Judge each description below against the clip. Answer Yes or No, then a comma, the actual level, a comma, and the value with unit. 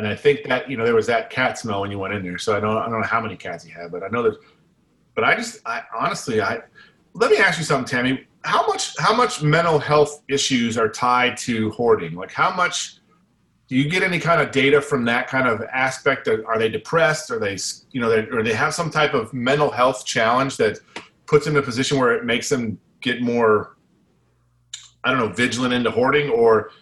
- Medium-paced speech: No, fast, 235 wpm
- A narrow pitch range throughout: No, average, 5.1 semitones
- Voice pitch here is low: Yes, low, 130 Hz